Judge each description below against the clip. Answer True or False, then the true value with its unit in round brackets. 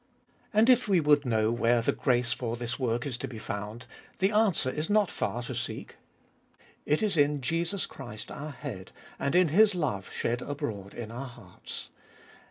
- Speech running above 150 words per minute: True (180 wpm)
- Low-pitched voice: True (130 Hz)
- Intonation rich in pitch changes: True (6.0 semitones)